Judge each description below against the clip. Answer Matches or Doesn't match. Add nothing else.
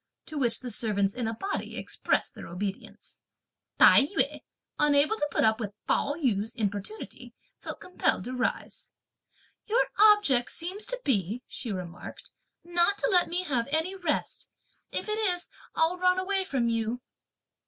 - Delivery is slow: Doesn't match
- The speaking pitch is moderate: Doesn't match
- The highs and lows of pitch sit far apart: Matches